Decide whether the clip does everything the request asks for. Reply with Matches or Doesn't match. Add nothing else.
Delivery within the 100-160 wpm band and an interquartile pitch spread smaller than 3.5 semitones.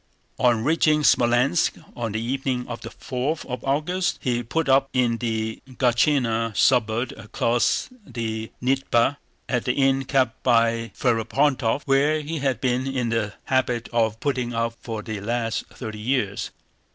Matches